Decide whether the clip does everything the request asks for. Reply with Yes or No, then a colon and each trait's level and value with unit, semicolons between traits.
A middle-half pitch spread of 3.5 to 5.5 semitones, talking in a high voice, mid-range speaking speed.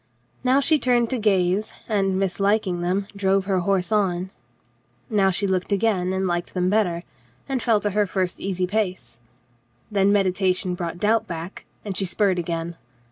No: narrow, 2.4 semitones; high, 195 Hz; average, 170 wpm